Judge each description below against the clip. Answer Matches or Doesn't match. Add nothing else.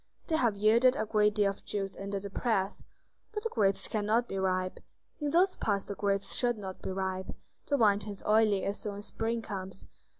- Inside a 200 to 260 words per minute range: Matches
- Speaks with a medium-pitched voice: Doesn't match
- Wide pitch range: Doesn't match